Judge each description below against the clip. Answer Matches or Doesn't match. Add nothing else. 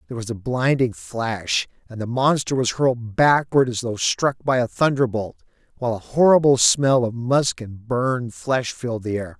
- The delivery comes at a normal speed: Matches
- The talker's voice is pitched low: Matches